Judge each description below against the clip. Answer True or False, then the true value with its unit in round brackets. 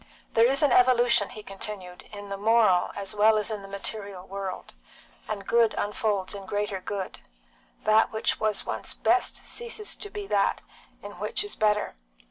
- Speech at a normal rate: True (170 wpm)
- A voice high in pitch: True (210 Hz)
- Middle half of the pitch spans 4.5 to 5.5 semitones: False (2.8 semitones)